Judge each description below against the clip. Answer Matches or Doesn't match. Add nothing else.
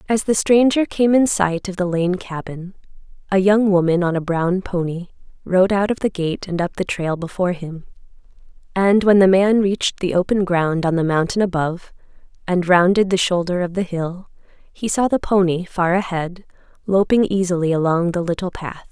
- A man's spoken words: Doesn't match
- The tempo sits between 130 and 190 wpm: Matches